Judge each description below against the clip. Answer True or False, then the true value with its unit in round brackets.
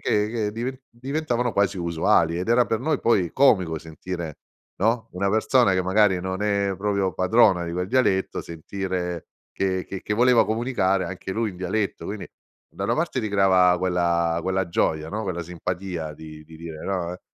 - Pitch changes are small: False (3.7 semitones)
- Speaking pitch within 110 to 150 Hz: False (95 Hz)